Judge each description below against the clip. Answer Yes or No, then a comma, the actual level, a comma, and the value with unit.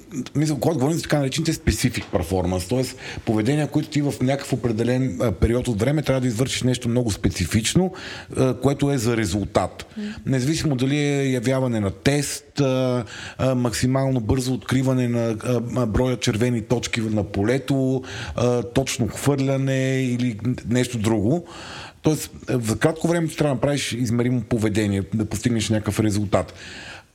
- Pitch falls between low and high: No, low, 125 Hz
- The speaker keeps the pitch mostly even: No, average, 3.3 semitones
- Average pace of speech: Yes, average, 135 wpm